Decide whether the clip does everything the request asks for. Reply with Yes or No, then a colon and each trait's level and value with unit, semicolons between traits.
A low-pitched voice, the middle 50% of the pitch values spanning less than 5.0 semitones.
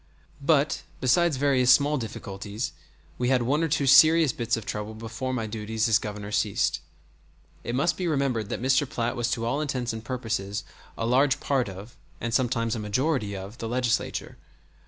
Yes: low, 120 Hz; average, 3.7 semitones